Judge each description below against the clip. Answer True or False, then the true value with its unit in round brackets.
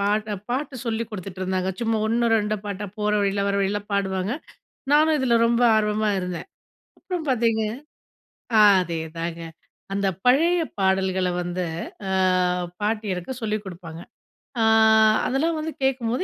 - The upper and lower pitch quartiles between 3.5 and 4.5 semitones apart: True (3.9 semitones)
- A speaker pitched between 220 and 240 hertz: False (210 Hz)